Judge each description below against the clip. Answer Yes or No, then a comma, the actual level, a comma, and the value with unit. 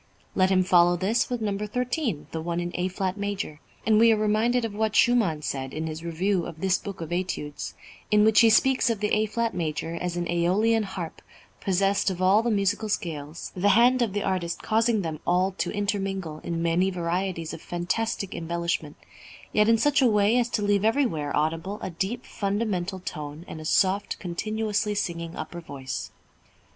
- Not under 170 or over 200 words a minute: Yes, average, 190 wpm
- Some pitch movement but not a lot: Yes, average, 4.0 semitones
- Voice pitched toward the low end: No, high, 190 Hz